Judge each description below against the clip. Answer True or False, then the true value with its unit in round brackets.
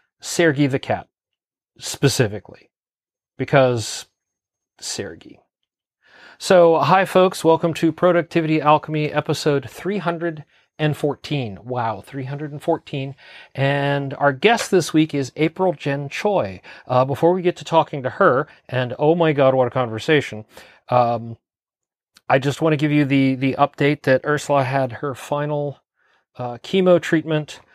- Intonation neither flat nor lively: True (3.5 semitones)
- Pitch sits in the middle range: True (145 Hz)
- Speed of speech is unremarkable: False (130 wpm)